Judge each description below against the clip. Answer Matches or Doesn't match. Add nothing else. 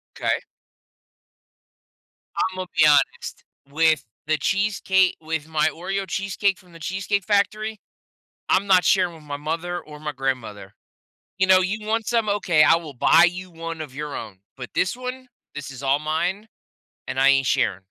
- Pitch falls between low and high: Matches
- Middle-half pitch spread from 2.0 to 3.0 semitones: Doesn't match